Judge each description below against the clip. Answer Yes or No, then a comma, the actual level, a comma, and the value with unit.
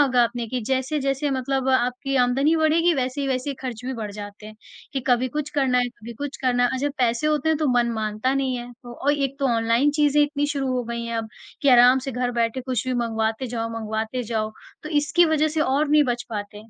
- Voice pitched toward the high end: Yes, very high, 255 Hz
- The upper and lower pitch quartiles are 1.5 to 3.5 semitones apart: Yes, average, 3.2 semitones